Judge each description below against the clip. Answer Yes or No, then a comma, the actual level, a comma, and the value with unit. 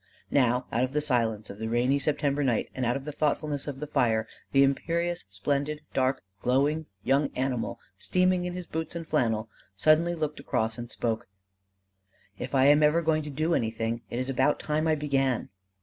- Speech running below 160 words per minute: No, average, 190 wpm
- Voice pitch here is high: No, medium, 140 Hz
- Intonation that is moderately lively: Yes, average, 3.9 semitones